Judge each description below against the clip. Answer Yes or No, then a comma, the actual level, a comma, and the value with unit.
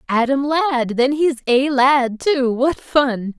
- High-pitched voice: Yes, very high, 265 Hz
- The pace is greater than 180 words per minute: No, average, 160 wpm